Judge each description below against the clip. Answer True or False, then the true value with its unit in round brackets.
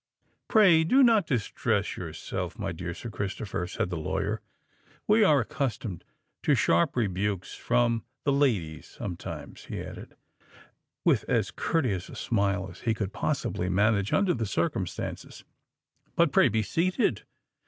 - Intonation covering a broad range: True (7.4 semitones)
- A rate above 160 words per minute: False (145 wpm)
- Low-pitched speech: True (110 Hz)